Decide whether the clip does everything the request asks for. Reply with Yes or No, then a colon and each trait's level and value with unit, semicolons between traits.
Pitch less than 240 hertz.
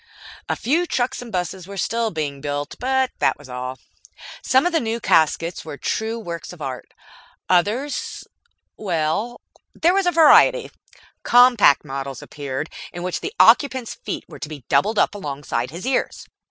Yes: high, 190 Hz